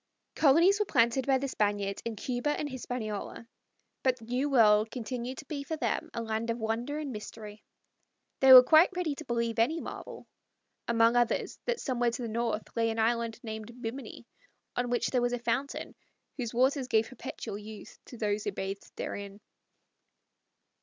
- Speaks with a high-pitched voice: Yes, high, 240 Hz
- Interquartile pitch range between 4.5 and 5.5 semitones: No, average, 3.0 semitones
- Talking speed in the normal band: Yes, average, 175 wpm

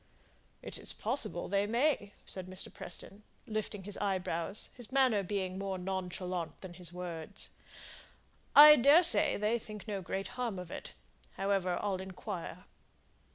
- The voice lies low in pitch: No, high, 195 Hz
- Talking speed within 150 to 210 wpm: No, average, 140 wpm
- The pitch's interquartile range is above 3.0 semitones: No, narrow, 2.6 semitones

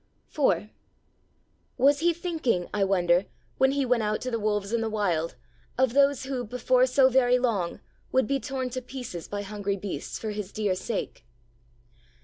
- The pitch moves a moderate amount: Yes, average, 4.4 semitones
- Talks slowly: No, average, 170 wpm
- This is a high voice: Yes, high, 235 Hz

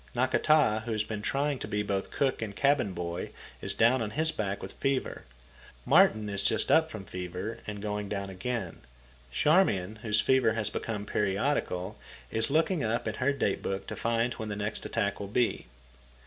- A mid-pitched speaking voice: No, low, 110 Hz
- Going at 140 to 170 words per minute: No, average, 185 wpm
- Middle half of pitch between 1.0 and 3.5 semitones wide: No, average, 4.1 semitones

